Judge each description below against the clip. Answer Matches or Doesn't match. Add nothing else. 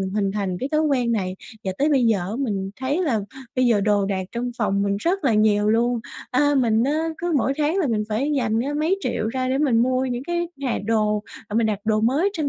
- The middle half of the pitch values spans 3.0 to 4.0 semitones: Doesn't match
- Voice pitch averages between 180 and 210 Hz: Doesn't match